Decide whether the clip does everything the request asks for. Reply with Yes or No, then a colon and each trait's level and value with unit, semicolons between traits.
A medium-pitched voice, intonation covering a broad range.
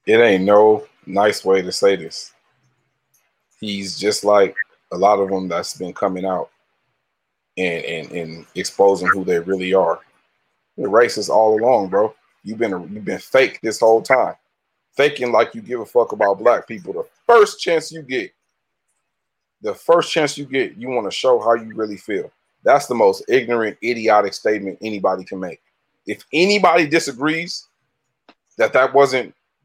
No: low, 110 Hz; wide, 8.6 semitones